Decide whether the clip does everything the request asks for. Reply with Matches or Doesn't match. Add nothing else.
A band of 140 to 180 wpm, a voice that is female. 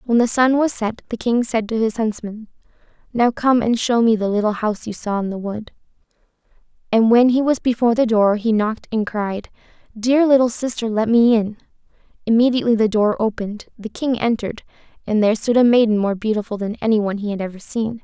Doesn't match